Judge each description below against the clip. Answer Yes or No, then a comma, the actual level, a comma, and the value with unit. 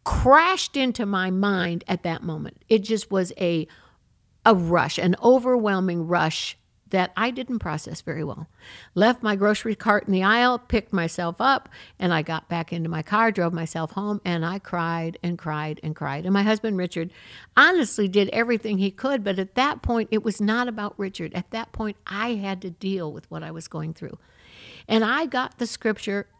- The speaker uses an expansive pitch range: No, average, 4.8 semitones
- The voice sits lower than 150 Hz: No, high, 195 Hz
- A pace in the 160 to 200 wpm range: Yes, average, 195 wpm